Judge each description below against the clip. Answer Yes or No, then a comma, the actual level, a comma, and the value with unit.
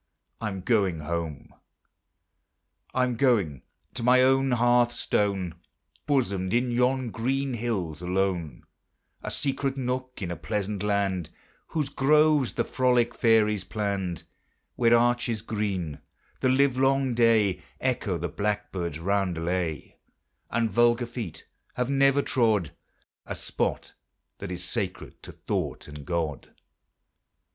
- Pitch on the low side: Yes, low, 110 Hz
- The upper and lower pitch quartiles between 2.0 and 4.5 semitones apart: No, wide, 5.5 semitones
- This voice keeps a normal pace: No, slow, 120 wpm